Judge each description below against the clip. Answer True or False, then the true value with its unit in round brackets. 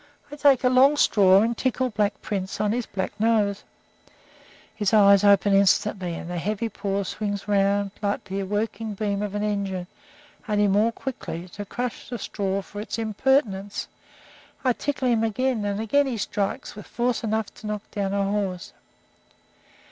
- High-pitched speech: True (205 Hz)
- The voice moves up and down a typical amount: False (2.3 semitones)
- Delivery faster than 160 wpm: True (170 wpm)